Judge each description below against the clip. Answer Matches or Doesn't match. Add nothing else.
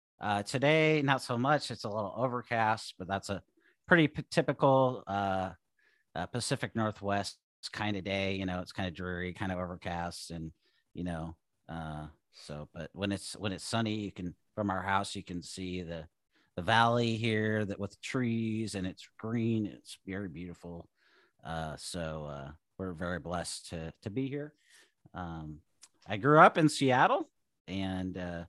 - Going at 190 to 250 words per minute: Doesn't match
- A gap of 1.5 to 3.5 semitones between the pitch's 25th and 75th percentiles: Doesn't match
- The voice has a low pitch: Matches